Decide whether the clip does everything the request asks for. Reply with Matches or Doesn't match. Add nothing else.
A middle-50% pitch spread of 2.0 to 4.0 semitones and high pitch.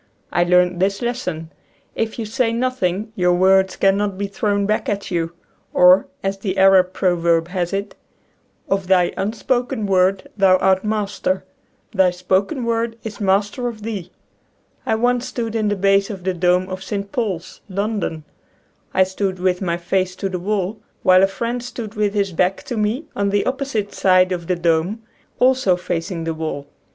Matches